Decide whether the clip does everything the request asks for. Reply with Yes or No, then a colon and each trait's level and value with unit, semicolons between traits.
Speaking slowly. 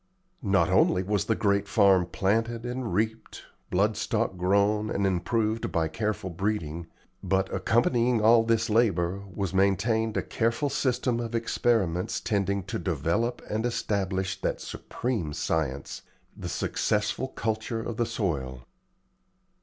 Yes: slow, 130 wpm